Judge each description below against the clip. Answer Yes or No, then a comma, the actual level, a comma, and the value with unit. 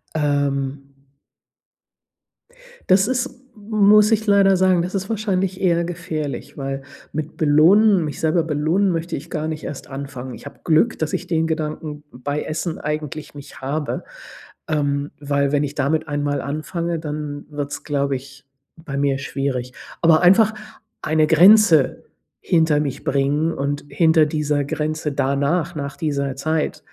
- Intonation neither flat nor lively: Yes, average, 3.2 semitones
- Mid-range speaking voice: Yes, medium, 155 Hz